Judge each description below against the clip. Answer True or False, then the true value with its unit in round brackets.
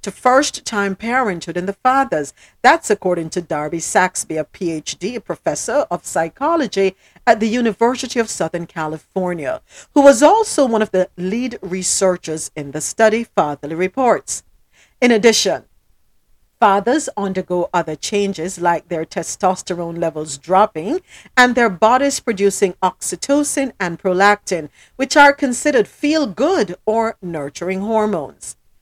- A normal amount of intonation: False (5.8 semitones)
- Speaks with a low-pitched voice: False (195 Hz)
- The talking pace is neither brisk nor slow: False (130 wpm)